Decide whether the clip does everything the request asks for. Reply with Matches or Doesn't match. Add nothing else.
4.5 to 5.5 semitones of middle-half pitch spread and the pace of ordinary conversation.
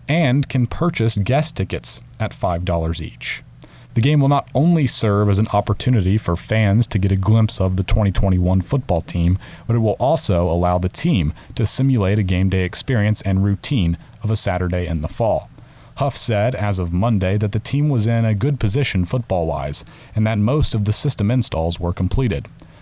Matches